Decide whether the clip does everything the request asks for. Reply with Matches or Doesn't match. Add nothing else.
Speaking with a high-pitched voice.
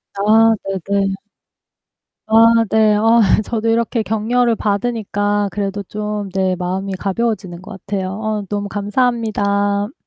Matches